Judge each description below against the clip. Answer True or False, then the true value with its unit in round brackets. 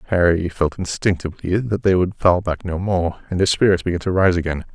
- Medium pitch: False (90 Hz)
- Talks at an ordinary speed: False (215 wpm)